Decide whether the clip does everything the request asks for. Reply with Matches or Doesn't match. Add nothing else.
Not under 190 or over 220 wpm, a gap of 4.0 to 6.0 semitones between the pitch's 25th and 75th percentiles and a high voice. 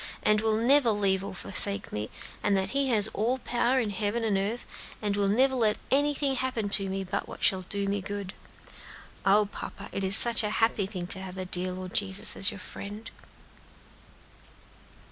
Doesn't match